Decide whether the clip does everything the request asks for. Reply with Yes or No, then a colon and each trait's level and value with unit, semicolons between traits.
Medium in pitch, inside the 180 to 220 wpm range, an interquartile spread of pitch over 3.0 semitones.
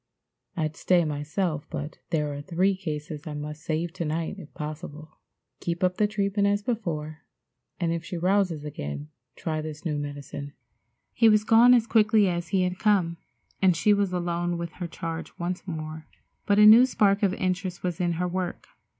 Yes: medium, 175 Hz; average, 185 wpm; average, 4.0 semitones